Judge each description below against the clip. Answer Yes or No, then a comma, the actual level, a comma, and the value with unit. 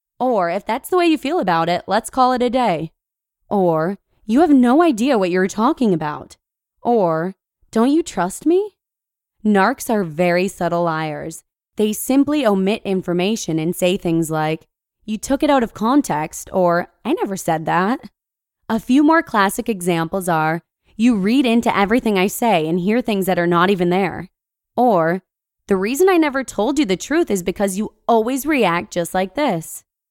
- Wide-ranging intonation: Yes, wide, 6.0 semitones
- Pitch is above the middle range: Yes, high, 200 Hz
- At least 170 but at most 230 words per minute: Yes, average, 175 wpm